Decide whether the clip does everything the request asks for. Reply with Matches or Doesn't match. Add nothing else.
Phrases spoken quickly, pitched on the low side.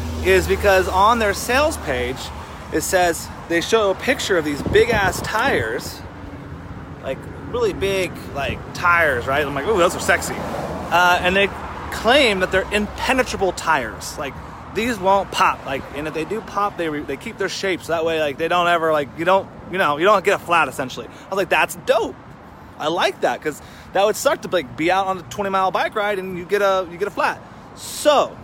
Doesn't match